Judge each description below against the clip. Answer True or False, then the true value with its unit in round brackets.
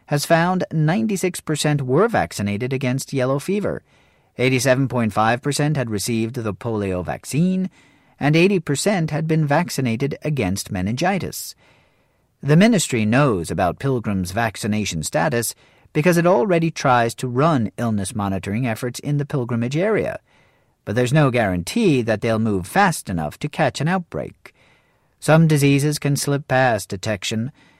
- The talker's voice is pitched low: True (130 Hz)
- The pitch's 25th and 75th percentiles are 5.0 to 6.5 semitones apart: True (5.6 semitones)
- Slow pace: True (130 wpm)